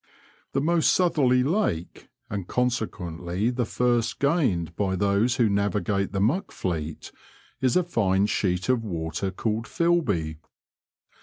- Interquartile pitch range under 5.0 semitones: No, wide, 5.5 semitones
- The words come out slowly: Yes, slow, 130 wpm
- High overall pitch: No, low, 105 Hz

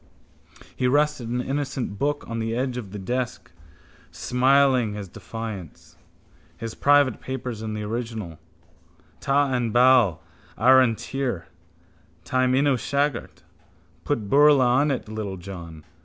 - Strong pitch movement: No, average, 4.0 semitones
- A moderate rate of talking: No, slow, 130 wpm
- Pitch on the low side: Yes, low, 125 Hz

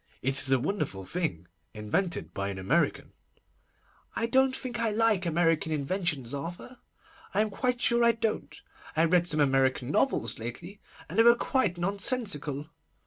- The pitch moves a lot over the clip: Yes, wide, 8.7 semitones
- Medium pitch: Yes, medium, 175 Hz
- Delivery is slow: No, average, 155 wpm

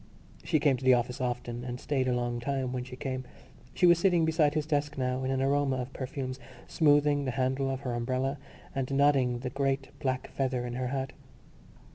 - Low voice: Yes, low, 130 Hz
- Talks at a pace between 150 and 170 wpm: No, fast, 205 wpm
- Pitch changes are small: Yes, narrow, 2.0 semitones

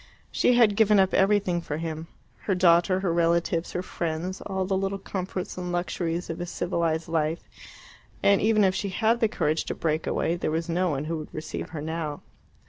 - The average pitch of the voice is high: No, medium, 175 Hz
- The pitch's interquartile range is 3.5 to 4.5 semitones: No, average, 2.7 semitones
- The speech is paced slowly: No, average, 200 wpm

